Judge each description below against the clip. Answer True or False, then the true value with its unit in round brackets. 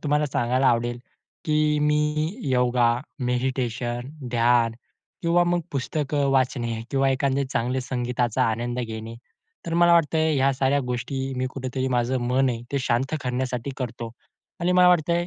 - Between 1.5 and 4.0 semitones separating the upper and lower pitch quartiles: True (2.8 semitones)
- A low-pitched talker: True (130 Hz)